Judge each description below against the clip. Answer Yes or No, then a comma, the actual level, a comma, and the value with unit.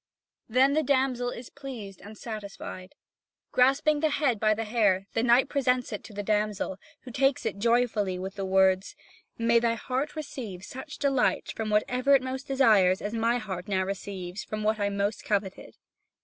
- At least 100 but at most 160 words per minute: No, average, 175 wpm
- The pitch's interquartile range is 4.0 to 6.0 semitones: Yes, average, 4.3 semitones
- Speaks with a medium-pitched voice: No, high, 225 Hz